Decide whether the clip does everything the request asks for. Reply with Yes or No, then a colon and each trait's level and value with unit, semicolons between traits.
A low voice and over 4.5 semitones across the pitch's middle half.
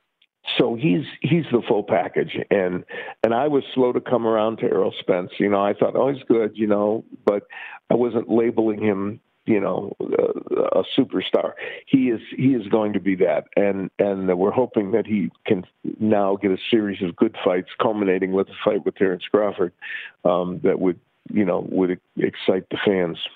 No: low, 110 Hz; average, 4.0 semitones